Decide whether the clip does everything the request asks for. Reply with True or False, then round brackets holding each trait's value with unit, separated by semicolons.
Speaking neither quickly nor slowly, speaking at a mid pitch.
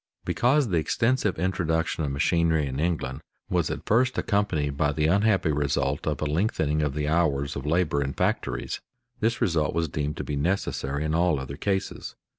False (180 wpm; 80 Hz)